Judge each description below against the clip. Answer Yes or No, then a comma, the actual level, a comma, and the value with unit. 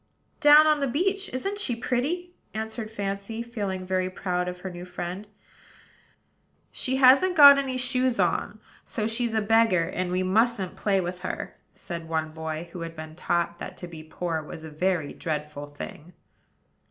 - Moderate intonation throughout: No, wide, 6.3 semitones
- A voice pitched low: No, high, 190 Hz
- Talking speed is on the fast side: No, average, 170 wpm